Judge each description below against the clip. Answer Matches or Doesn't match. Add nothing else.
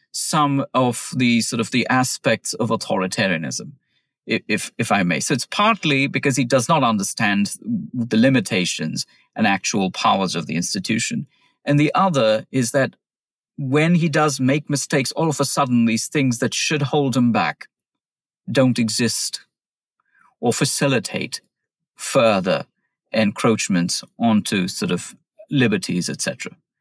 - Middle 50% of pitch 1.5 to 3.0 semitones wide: Doesn't match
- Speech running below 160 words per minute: Matches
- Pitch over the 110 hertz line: Matches